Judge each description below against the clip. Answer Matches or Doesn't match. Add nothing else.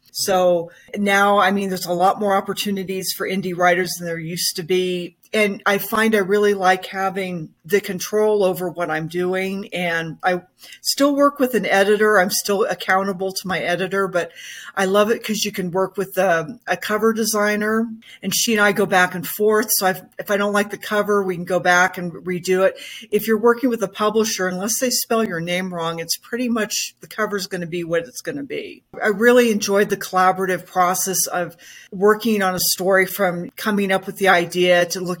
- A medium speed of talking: Doesn't match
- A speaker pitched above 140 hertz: Matches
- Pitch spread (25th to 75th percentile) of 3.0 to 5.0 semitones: Doesn't match